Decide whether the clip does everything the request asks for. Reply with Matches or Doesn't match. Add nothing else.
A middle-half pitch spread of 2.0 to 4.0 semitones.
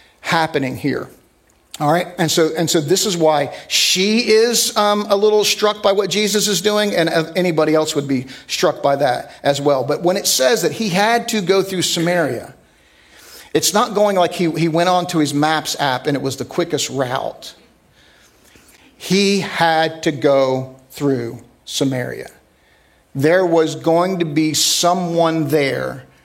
Doesn't match